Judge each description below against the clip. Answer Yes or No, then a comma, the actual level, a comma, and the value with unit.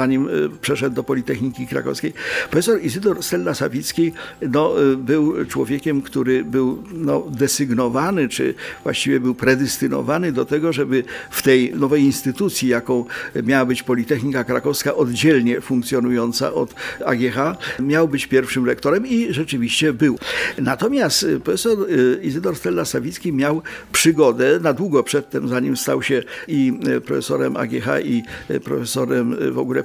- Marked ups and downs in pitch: No, average, 3.4 semitones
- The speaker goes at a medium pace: Yes, average, 125 wpm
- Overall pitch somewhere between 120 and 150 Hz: Yes, low, 135 Hz